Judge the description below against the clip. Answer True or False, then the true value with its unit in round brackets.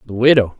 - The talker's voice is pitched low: True (115 Hz)